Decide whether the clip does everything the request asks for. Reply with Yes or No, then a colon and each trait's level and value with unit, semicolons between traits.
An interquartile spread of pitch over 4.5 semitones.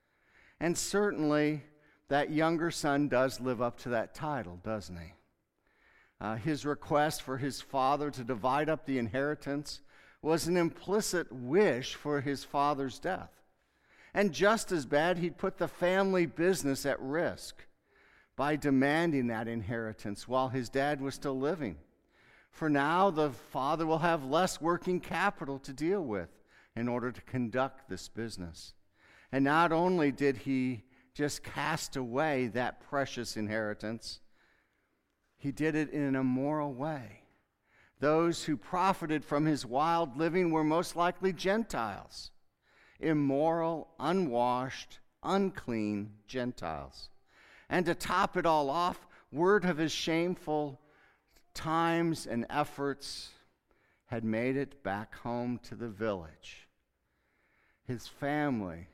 Yes: average, 4.9 semitones